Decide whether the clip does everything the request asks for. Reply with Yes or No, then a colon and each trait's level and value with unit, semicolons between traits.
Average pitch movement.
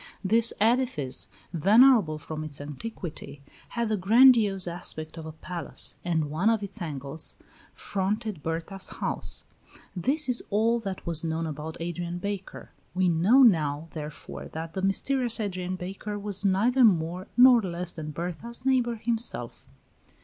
No: wide, 5.7 semitones